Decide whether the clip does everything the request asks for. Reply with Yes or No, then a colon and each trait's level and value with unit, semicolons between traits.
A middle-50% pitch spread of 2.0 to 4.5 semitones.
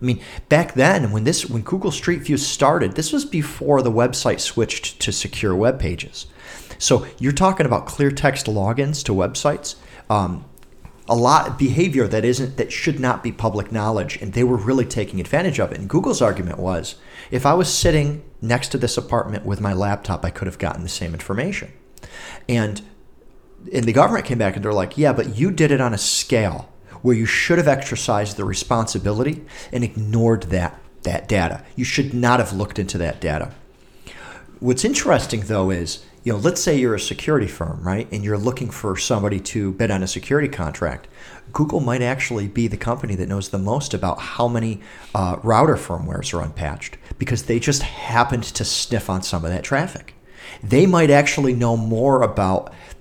No: average, 5.2 semitones